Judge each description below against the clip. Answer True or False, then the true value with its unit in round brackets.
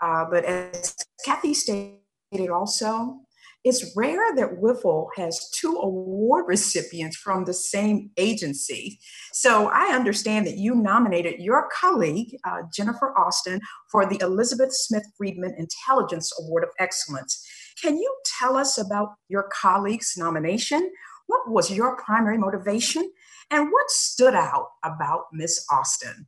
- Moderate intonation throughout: False (6.3 semitones)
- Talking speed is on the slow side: True (130 wpm)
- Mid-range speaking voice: False (210 Hz)